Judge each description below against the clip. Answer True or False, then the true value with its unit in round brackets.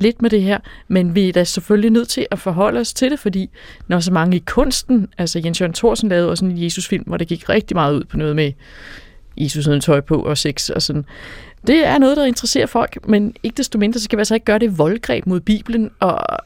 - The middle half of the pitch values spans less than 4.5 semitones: False (5.1 semitones)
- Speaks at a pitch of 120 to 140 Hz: False (195 Hz)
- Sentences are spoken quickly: True (250 wpm)